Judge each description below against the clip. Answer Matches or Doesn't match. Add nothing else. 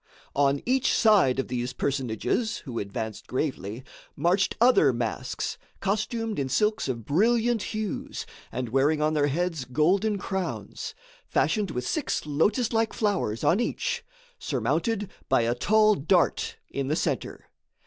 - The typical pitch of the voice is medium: Matches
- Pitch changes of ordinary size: Doesn't match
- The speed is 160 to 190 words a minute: Doesn't match